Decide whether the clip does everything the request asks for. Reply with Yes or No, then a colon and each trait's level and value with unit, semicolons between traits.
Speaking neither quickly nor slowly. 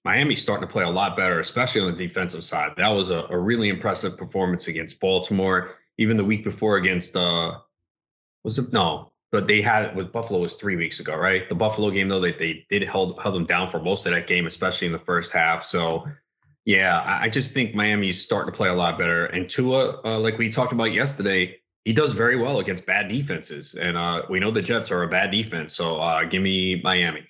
No: fast, 230 wpm